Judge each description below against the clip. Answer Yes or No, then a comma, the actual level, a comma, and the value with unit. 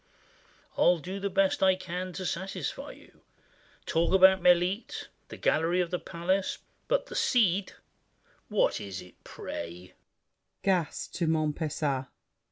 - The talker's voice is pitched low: No, medium, 185 Hz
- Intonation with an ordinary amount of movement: No, narrow, 2.2 semitones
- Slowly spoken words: Yes, slow, 115 wpm